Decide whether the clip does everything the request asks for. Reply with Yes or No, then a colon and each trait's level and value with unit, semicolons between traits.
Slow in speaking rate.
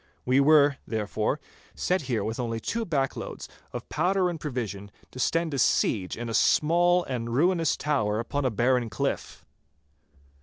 No: average, 155 wpm